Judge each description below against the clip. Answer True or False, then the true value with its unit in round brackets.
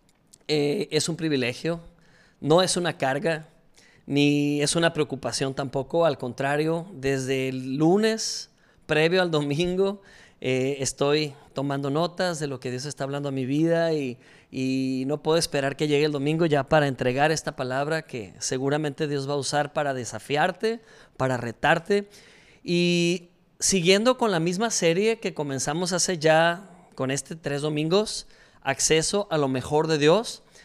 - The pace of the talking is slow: False (155 wpm)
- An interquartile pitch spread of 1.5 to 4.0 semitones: True (3.7 semitones)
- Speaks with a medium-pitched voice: True (155 Hz)